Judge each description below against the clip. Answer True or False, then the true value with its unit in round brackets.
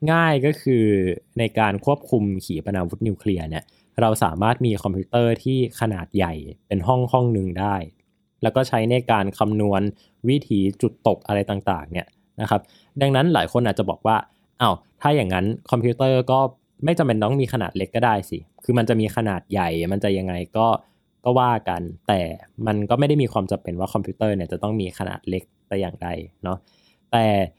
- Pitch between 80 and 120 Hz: True (105 Hz)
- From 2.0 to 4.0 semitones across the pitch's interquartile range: False (4.4 semitones)